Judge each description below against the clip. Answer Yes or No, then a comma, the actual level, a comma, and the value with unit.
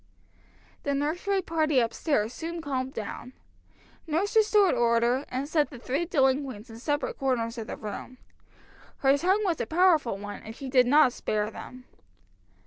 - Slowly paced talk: No, average, 160 wpm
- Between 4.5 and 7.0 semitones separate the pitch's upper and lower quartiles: Yes, average, 5.2 semitones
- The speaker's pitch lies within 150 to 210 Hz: No, very high, 270 Hz